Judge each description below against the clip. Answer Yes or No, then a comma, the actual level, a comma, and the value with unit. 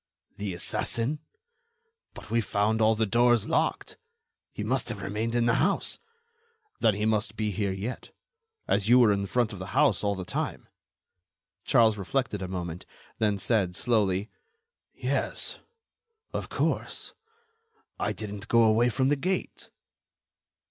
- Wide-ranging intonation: No, average, 2.8 semitones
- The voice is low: Yes, low, 110 Hz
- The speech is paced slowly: No, average, 145 wpm